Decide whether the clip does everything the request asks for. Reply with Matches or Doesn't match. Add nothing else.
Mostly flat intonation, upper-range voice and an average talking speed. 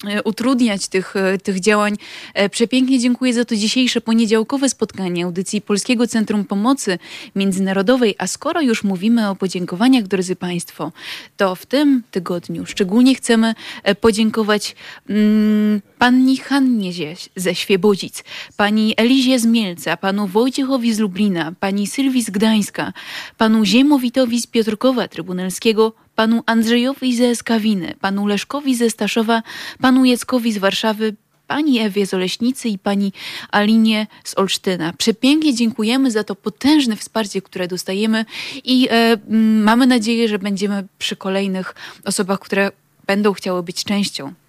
Doesn't match